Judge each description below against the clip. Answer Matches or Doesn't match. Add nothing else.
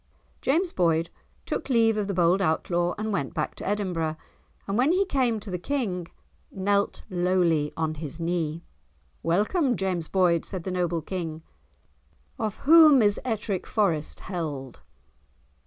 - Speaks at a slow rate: Doesn't match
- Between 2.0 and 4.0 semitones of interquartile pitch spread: Doesn't match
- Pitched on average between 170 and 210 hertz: Matches